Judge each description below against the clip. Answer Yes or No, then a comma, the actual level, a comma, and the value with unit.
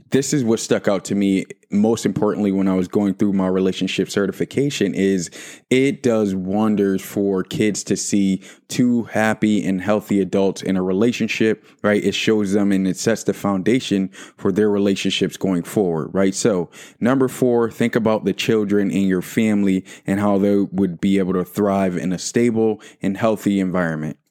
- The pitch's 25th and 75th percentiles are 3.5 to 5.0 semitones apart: No, narrow, 2.4 semitones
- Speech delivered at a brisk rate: No, average, 180 wpm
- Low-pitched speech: Yes, low, 100 Hz